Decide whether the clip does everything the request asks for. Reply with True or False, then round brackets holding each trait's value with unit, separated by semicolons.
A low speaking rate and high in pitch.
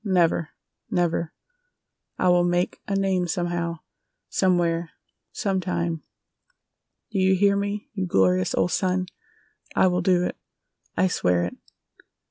False (125 wpm; 180 Hz)